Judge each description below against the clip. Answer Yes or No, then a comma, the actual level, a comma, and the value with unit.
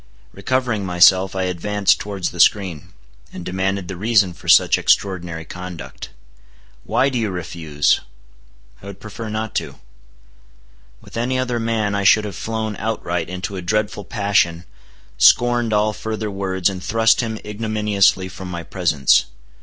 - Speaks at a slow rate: No, average, 145 wpm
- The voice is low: Yes, low, 100 Hz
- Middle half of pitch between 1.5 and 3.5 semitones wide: Yes, average, 3.2 semitones